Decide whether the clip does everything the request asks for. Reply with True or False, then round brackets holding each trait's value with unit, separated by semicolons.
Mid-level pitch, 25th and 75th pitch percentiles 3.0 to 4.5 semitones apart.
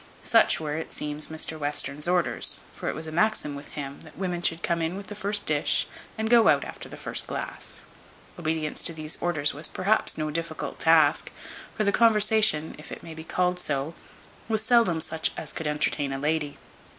True (160 Hz; 3.5 semitones)